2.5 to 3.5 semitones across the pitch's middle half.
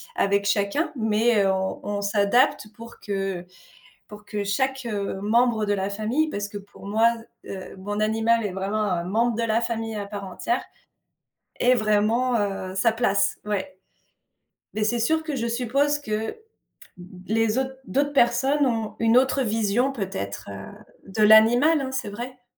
Yes: average, 3.2 semitones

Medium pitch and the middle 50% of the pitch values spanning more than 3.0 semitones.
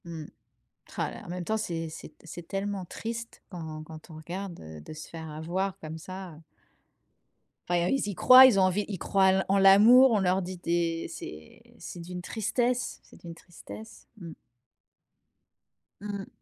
Yes: medium, 180 Hz; average, 3.4 semitones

